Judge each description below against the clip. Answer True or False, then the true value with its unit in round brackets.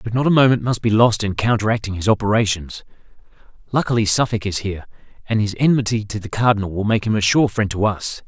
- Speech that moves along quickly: True (210 wpm)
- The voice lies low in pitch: True (110 Hz)